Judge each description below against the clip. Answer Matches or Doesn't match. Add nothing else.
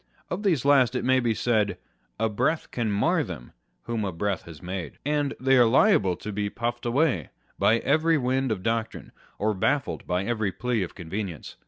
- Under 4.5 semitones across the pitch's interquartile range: Doesn't match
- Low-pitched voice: Matches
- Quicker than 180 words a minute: Matches